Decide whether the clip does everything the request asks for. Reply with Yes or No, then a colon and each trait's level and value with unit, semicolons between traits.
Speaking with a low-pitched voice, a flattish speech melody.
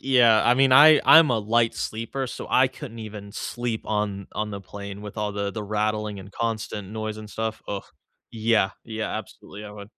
Yes: low, 110 Hz; narrow, 2.1 semitones